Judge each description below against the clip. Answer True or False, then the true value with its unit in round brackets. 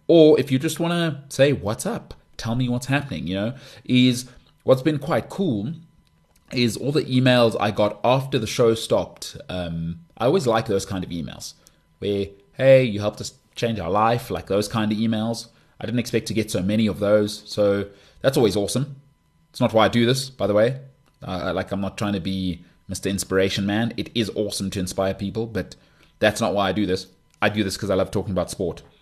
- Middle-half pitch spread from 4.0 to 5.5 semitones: True (4.4 semitones)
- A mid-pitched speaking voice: False (110 Hz)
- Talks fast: True (215 wpm)